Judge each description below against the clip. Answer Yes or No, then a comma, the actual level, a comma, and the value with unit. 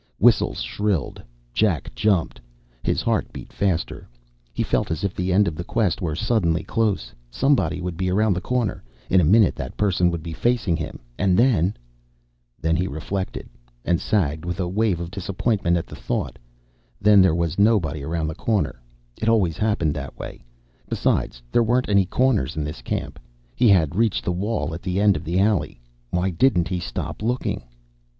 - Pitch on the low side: Yes, very low, 90 Hz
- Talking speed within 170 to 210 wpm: Yes, average, 185 wpm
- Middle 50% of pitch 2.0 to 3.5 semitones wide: No, average, 4.2 semitones